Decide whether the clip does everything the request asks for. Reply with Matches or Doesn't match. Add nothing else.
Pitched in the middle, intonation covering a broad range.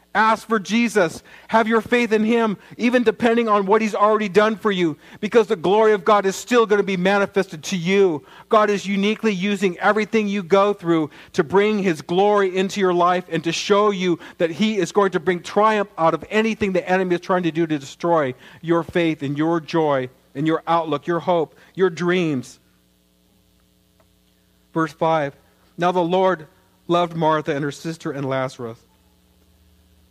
Doesn't match